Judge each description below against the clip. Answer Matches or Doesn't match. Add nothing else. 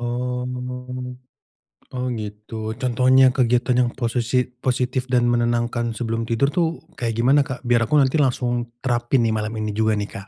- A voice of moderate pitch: Doesn't match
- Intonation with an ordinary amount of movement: Doesn't match